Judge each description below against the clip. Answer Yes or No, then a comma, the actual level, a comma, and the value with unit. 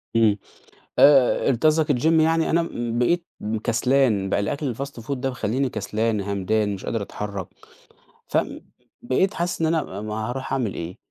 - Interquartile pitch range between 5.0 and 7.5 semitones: Yes, wide, 5.4 semitones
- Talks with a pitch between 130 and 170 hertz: No, low, 120 Hz